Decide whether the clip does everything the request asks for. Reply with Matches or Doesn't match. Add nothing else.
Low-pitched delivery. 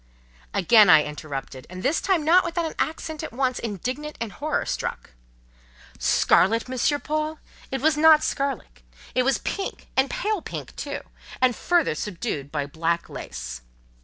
Doesn't match